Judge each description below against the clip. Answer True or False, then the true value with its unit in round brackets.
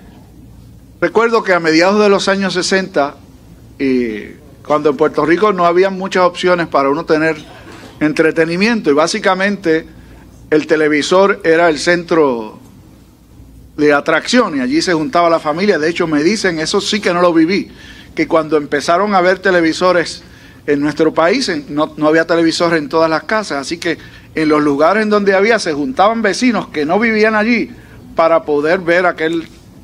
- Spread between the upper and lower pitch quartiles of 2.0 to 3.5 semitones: False (4.0 semitones)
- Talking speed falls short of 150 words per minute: False (165 wpm)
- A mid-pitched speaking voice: True (165 Hz)